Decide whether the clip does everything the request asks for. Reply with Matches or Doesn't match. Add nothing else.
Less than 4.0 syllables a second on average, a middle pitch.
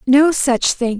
Doesn't match